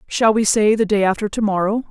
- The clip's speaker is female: Yes, female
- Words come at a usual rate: No, fast, 250 wpm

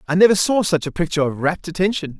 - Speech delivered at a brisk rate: Yes, fast, 245 wpm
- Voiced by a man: Yes, male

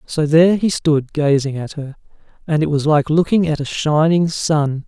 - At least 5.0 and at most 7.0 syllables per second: No, 4.7 syllables/s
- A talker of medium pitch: Yes, medium, 155 Hz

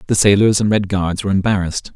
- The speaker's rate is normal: No, fast, 215 wpm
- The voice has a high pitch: No, low, 100 Hz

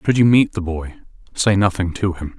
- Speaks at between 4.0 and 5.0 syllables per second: No, 5.4 syllables/s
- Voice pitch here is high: No, very low, 95 Hz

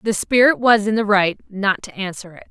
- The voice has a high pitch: Yes, high, 200 Hz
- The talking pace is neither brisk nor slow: No, fast, 240 wpm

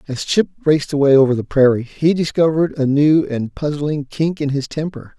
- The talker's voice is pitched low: No, medium, 145 Hz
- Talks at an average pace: Yes, average, 195 wpm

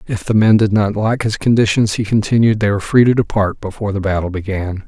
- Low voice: Yes, low, 105 Hz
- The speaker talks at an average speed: No, fast, 235 wpm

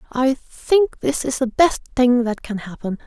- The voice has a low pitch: No, very high, 255 Hz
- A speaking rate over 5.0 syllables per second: No, 4.4 syllables/s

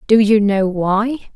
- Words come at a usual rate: Yes, average, 175 wpm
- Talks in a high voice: Yes, high, 210 Hz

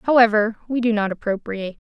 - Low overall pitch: No, high, 220 Hz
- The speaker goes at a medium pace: Yes, average, 160 wpm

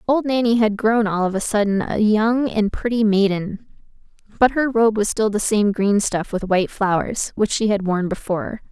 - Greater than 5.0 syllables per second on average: No, 4.9 syllables/s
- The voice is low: No, high, 210 Hz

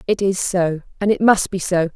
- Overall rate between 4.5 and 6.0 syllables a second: Yes, 5.0 syllables/s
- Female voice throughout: Yes, female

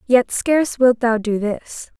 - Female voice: Yes, female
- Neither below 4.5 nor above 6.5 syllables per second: No, 3.9 syllables/s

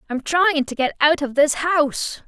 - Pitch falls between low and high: No, very high, 295 Hz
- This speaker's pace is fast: Yes, fast, 210 wpm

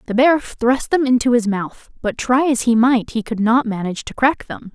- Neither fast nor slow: No, fast, 240 wpm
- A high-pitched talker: Yes, high, 240 Hz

